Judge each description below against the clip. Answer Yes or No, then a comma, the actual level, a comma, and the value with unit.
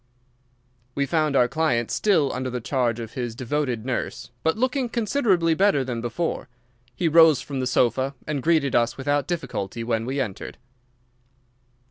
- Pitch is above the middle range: No, low, 135 Hz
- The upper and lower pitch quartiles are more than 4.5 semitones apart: Yes, average, 5.0 semitones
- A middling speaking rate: Yes, average, 155 wpm